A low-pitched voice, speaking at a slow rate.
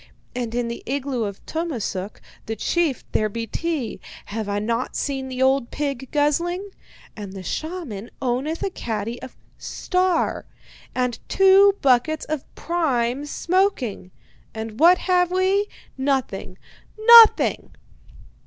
No: very high, 270 Hz; slow, 125 wpm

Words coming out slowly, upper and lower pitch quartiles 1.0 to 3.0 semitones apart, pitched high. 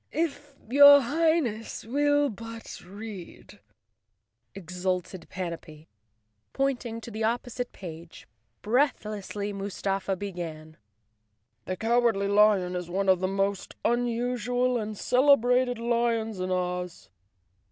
No: slow, 100 wpm; average, 4.7 semitones; high, 215 Hz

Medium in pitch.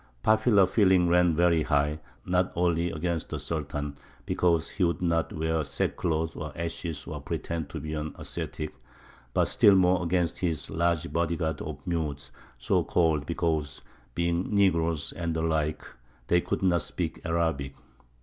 No: very low, 85 Hz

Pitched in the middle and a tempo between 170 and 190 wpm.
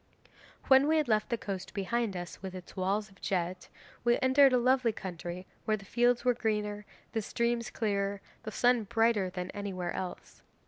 No: high, 210 Hz; average, 185 wpm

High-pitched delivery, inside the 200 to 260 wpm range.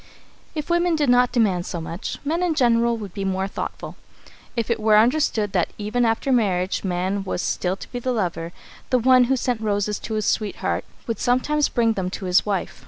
Yes: high, 220 Hz; fast, 205 wpm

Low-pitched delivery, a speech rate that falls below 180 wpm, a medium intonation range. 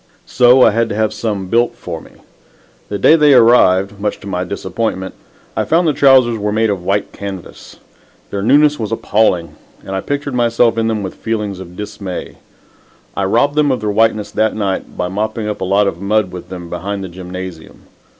No: low, 105 Hz; average, 200 wpm; average, 3.4 semitones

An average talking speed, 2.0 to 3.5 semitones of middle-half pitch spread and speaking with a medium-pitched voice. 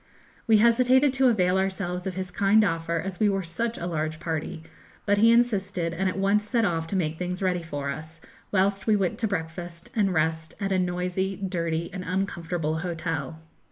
Yes: average, 195 wpm; average, 3.2 semitones; medium, 180 Hz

